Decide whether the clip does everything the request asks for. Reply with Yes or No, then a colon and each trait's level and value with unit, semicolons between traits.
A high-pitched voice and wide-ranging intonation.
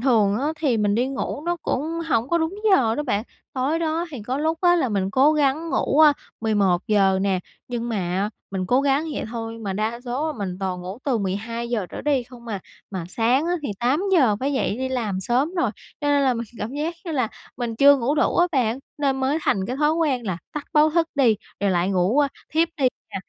Yes: very high, 250 Hz; wide, 5.7 semitones